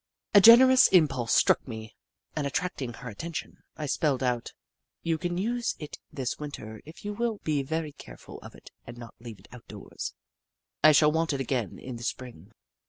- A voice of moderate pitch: Yes, medium, 145 Hz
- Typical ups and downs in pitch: No, wide, 5.7 semitones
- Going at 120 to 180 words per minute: No, average, 190 wpm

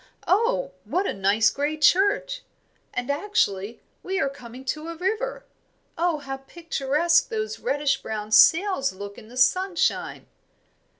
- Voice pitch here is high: Yes, very high, 305 Hz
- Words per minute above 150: No, slow, 135 wpm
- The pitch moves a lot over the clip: Yes, wide, 7.3 semitones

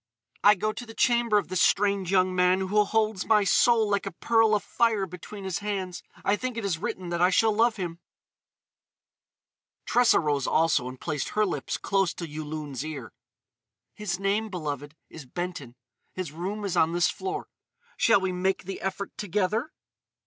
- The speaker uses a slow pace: No, average, 175 wpm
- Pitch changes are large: No, average, 3.7 semitones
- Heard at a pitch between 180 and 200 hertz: Yes, high, 190 Hz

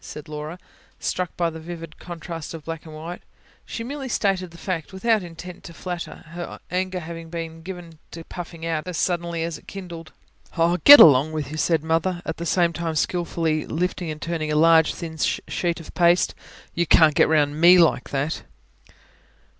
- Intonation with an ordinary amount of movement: No, narrow, 1.8 semitones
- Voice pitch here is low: No, medium, 165 Hz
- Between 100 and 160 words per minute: No, average, 185 wpm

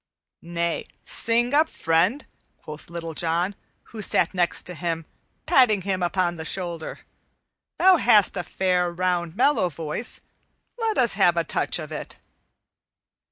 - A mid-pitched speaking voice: Yes, medium, 180 Hz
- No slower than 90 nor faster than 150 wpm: Yes, average, 140 wpm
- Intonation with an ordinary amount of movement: Yes, average, 4.3 semitones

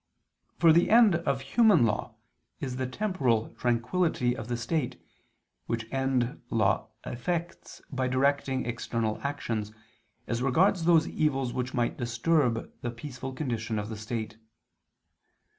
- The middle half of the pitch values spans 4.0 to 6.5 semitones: Yes, average, 4.7 semitones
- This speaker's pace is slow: Yes, slow, 130 wpm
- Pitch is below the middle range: Yes, low, 125 Hz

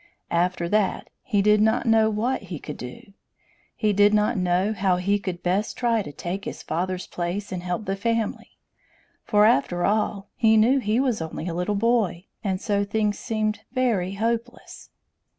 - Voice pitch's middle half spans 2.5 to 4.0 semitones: Yes, average, 3.3 semitones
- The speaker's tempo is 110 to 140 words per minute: No, average, 175 wpm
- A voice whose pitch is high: Yes, high, 205 Hz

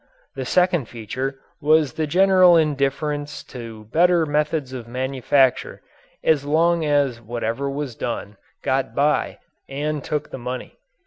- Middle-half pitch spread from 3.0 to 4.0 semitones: Yes, average, 3.4 semitones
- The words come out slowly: Yes, slow, 130 wpm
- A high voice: No, medium, 140 Hz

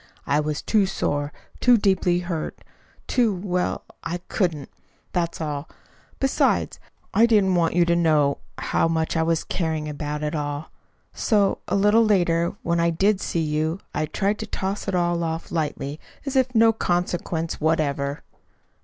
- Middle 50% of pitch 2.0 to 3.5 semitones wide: No, average, 4.0 semitones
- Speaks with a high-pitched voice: No, medium, 170 Hz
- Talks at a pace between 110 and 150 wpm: No, average, 160 wpm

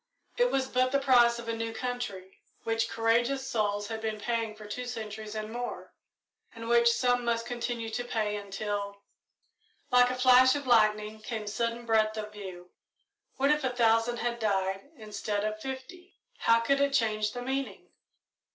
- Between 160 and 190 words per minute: Yes, average, 170 wpm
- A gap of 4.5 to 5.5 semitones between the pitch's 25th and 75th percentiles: No, narrow, 2.5 semitones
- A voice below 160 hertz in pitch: No, high, 230 Hz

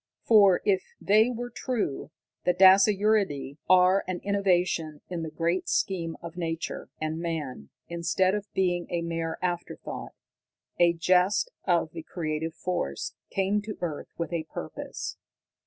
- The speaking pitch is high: No, medium, 175 Hz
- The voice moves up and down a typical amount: Yes, average, 3.1 semitones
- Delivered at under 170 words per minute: Yes, average, 140 wpm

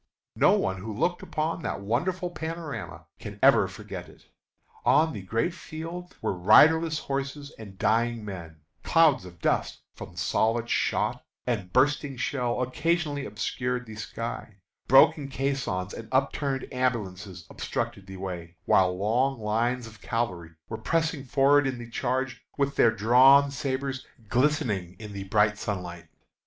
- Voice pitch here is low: Yes, low, 125 Hz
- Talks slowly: No, average, 145 wpm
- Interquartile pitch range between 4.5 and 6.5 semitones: Yes, average, 5.3 semitones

